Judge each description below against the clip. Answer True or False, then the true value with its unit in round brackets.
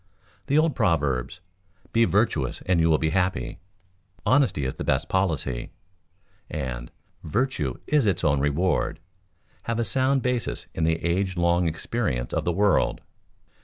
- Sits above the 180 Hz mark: False (90 Hz)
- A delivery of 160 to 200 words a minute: False (145 wpm)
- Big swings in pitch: True (7.6 semitones)